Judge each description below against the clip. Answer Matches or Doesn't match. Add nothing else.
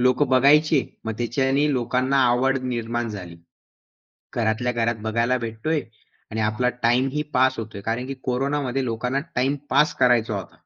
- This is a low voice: Matches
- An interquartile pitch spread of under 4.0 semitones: Matches